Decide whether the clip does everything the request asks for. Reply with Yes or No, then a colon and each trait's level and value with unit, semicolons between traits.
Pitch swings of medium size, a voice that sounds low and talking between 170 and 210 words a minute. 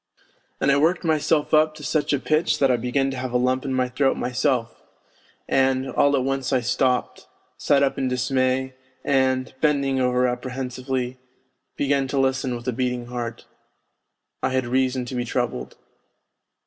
No: narrow, 1.6 semitones; low, 130 Hz; average, 175 wpm